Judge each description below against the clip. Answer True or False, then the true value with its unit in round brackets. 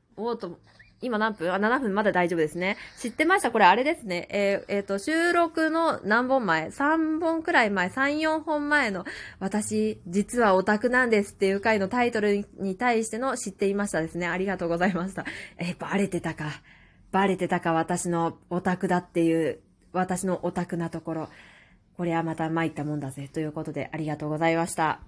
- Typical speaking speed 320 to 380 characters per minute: True (370 characters per minute)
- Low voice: False (185 Hz)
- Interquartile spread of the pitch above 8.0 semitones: False (5.2 semitones)